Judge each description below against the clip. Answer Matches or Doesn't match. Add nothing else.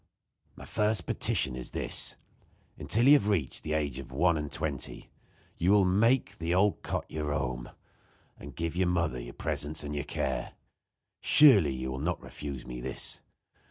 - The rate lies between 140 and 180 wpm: Matches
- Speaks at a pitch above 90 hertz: Doesn't match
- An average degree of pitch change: Doesn't match